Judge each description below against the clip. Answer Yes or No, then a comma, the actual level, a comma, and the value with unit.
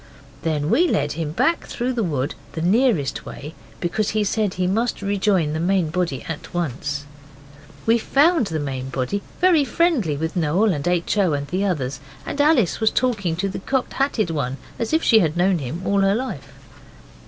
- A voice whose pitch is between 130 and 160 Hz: No, medium, 185 Hz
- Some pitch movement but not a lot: No, wide, 6.5 semitones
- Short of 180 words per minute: No, average, 190 wpm